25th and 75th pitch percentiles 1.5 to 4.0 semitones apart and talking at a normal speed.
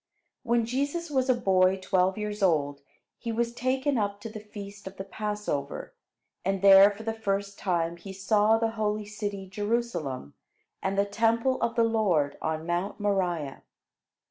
Yes: average, 3.1 semitones; average, 165 wpm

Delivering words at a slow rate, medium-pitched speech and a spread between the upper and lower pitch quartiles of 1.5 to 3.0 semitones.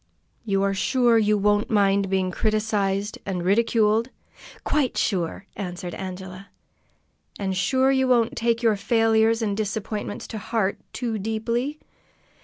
No: slow, 130 wpm; high, 210 Hz; average, 2.7 semitones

